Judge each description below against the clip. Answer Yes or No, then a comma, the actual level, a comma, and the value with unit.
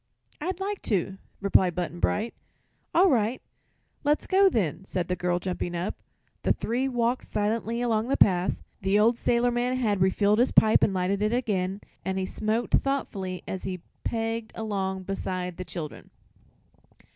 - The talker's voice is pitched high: Yes, high, 210 Hz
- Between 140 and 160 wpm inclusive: Yes, average, 155 wpm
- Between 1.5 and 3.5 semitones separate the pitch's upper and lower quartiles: No, average, 4.2 semitones